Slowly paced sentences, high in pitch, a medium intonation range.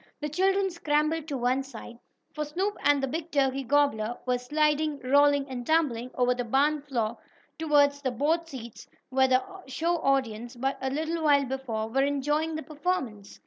No: average, 175 wpm; very high, 280 Hz; average, 3.2 semitones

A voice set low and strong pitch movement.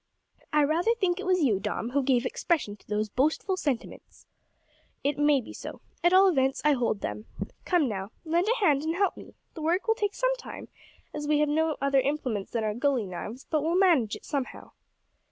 No: very high, 295 Hz; wide, 5.7 semitones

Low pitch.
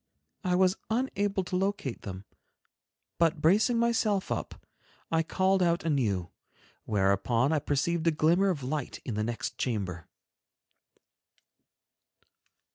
No: medium, 165 Hz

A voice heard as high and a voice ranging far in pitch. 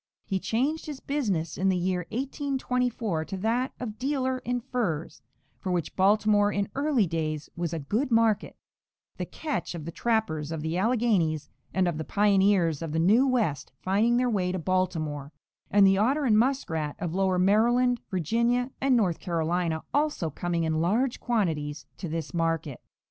Yes: high, 195 Hz; wide, 6.5 semitones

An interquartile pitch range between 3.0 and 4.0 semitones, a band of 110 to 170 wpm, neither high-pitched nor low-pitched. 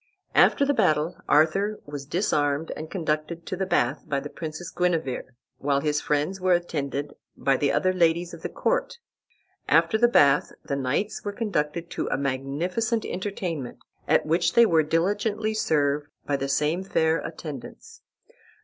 No: average, 4.4 semitones; average, 160 wpm; medium, 160 Hz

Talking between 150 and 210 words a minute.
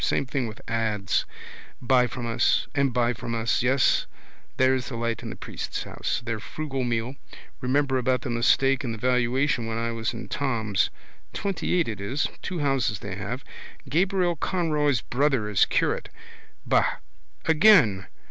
Yes: average, 155 wpm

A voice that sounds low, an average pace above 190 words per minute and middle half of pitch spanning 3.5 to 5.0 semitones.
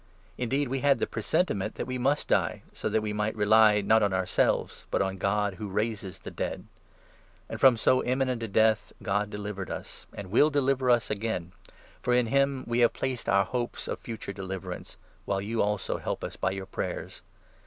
Yes: low, 110 Hz; average, 200 wpm; average, 4.1 semitones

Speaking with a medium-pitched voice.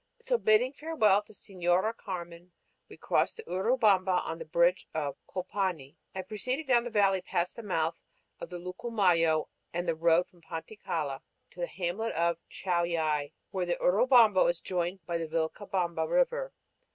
Yes: medium, 180 Hz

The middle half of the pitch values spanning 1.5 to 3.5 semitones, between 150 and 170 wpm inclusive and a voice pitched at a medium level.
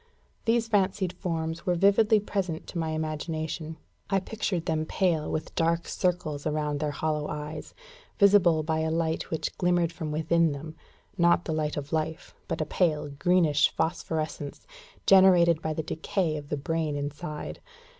Yes: narrow, 2.4 semitones; average, 155 wpm; medium, 160 Hz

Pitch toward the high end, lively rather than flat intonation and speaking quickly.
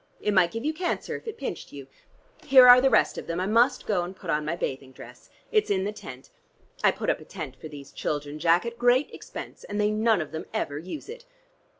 Yes: high, 200 Hz; wide, 7.8 semitones; fast, 245 wpm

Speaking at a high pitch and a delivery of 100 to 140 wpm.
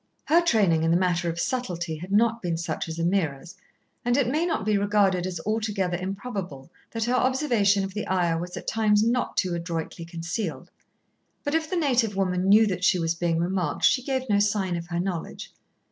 No: high, 195 Hz; average, 200 wpm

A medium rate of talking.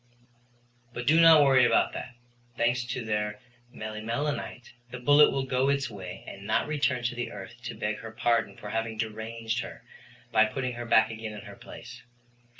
Yes: average, 180 wpm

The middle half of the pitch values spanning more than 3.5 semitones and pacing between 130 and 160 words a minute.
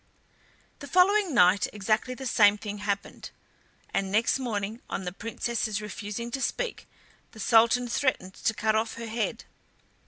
No: average, 3.0 semitones; average, 150 wpm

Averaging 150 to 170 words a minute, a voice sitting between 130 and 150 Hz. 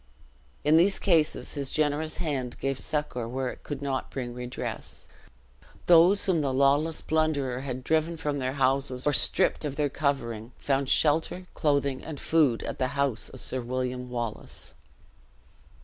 Yes: average, 155 wpm; medium, 140 Hz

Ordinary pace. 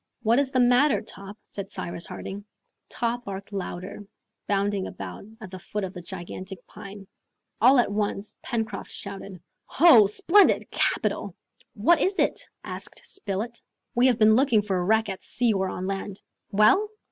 Yes: average, 160 wpm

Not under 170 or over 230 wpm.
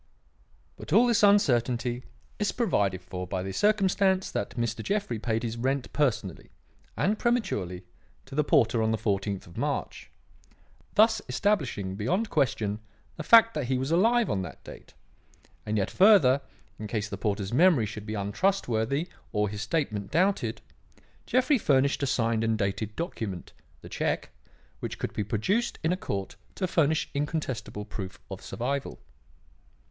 No: average, 155 wpm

